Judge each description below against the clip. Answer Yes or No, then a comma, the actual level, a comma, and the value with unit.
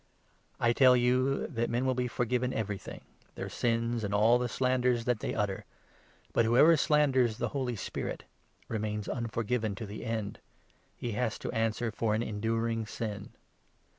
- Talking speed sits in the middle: Yes, average, 170 wpm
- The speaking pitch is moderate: No, low, 115 Hz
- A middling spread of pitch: No, narrow, 2.2 semitones